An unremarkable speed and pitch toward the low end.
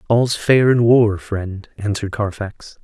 Yes: average, 150 wpm; low, 105 Hz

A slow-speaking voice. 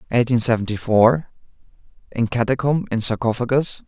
Yes: slow, 95 wpm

